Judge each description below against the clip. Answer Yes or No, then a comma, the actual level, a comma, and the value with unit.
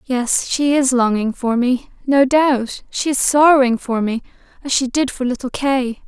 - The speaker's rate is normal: Yes, average, 190 wpm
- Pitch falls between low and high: No, very high, 260 Hz